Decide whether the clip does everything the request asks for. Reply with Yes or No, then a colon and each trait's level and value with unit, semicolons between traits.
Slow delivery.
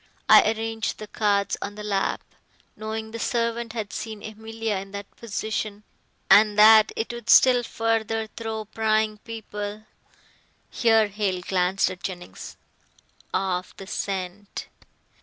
Yes: slow, 130 wpm